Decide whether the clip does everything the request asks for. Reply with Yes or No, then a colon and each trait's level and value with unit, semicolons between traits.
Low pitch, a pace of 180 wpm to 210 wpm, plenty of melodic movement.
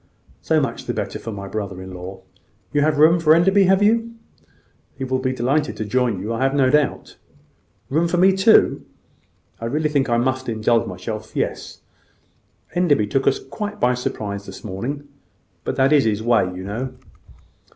Yes: low, 130 Hz; average, 185 wpm; wide, 6.0 semitones